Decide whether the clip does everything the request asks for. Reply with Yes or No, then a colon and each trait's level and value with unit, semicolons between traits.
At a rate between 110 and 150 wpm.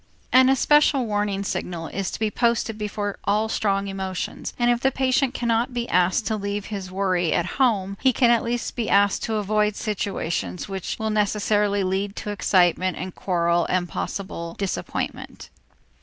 No: average, 170 wpm